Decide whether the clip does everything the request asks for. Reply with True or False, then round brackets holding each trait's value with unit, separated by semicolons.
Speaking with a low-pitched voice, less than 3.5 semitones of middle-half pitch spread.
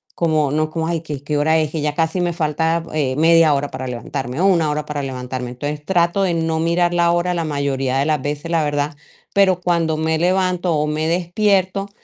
False (160 Hz; 2.7 semitones)